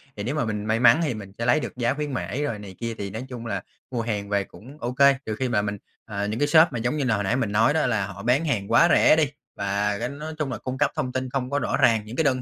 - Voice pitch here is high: No, low, 120 Hz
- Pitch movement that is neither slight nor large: Yes, average, 4.7 semitones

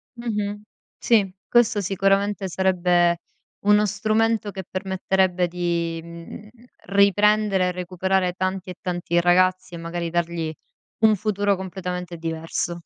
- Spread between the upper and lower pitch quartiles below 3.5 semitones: Yes, narrow, 2.6 semitones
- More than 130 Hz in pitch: Yes, medium, 185 Hz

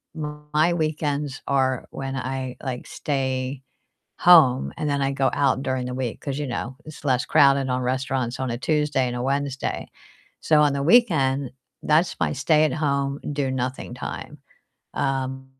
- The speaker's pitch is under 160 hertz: Yes, low, 135 Hz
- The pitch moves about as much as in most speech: No, narrow, 2.2 semitones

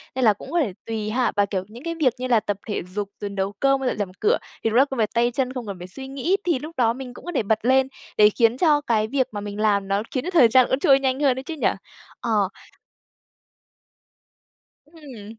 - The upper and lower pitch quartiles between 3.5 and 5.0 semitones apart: Yes, average, 4.4 semitones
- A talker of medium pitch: No, high, 240 Hz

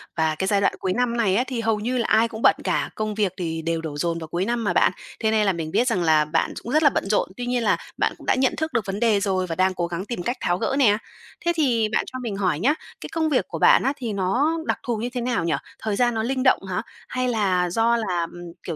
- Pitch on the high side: Yes, high, 215 Hz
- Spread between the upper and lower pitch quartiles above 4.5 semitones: Yes, average, 5.2 semitones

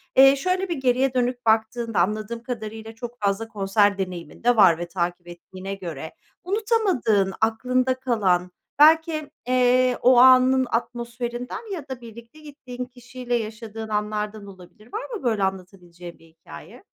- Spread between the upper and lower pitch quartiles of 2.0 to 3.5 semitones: No, average, 4.4 semitones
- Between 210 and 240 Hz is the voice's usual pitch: Yes, high, 230 Hz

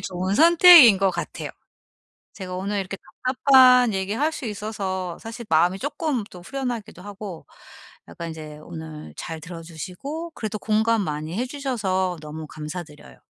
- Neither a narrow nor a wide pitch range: No, wide, 6.3 semitones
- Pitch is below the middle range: No, high, 195 Hz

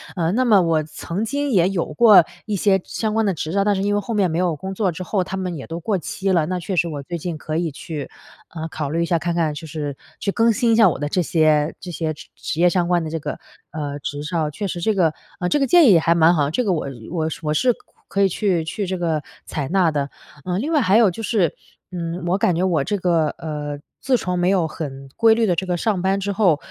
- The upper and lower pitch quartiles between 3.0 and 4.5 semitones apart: Yes, average, 3.9 semitones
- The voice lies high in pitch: No, medium, 175 Hz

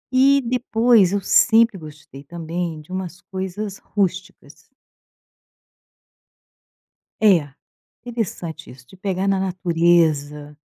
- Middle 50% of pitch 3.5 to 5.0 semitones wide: Yes, average, 4.2 semitones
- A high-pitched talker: No, medium, 180 Hz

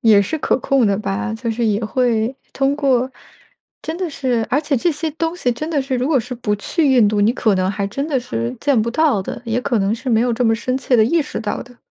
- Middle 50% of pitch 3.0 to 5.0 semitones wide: Yes, average, 4.1 semitones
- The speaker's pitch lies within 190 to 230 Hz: No, high, 245 Hz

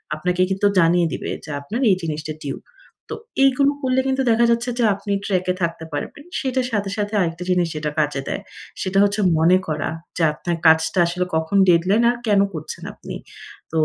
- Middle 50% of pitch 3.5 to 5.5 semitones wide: Yes, average, 4.7 semitones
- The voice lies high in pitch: No, medium, 180 Hz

